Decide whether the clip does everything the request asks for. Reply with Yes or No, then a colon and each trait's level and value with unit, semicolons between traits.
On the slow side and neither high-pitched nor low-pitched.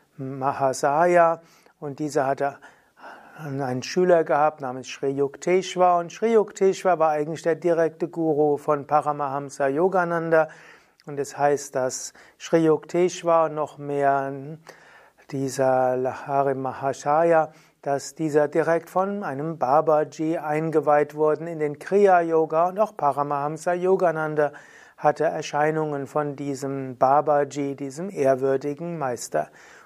Yes: slow, 115 wpm; medium, 150 Hz